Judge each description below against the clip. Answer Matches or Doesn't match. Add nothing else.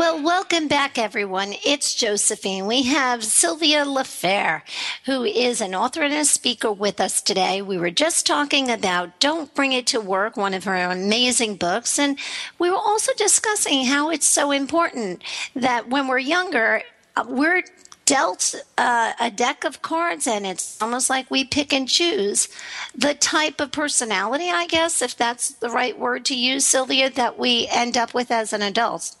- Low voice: Doesn't match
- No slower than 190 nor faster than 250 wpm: Doesn't match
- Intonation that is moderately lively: Matches